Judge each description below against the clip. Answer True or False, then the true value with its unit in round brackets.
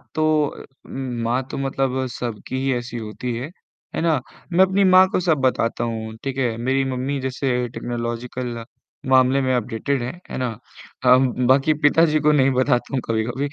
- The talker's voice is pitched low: True (130 Hz)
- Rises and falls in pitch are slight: True (2.3 semitones)